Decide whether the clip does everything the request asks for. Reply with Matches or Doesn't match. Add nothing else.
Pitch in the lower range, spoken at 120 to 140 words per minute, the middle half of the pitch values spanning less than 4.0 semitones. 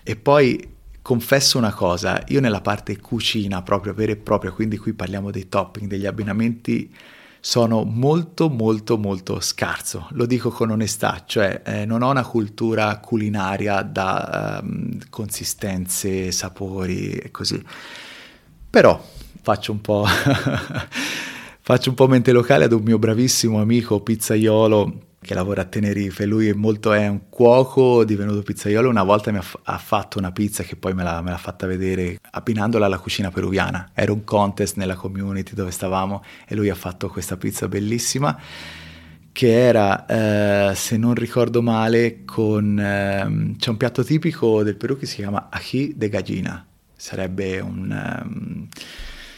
Doesn't match